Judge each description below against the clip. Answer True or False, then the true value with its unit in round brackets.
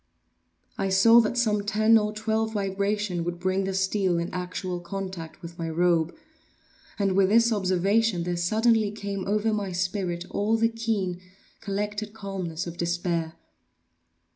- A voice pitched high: True (195 Hz)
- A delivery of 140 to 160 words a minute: True (145 wpm)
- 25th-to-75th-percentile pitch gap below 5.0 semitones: True (3.2 semitones)